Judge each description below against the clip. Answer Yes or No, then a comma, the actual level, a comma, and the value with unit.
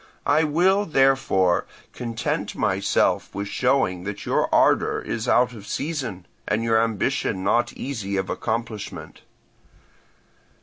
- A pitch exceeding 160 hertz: No, low, 115 Hz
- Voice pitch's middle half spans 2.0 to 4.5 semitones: No, average, 5.1 semitones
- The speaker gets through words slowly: Yes, slow, 120 wpm